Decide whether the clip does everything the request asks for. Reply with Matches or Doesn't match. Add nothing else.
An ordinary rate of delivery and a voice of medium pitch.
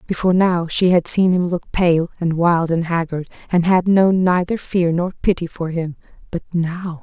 Matches